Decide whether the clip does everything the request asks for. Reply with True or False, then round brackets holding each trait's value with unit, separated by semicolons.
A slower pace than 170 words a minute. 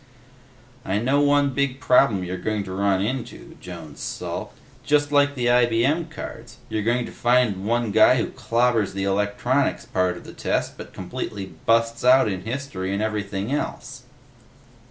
True (160 wpm)